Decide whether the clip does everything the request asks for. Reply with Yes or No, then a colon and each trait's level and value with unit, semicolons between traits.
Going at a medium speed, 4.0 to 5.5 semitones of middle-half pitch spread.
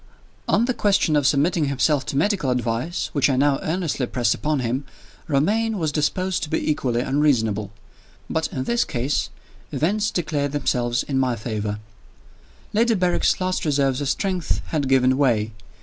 Yes: average, 165 wpm; average, 5.2 semitones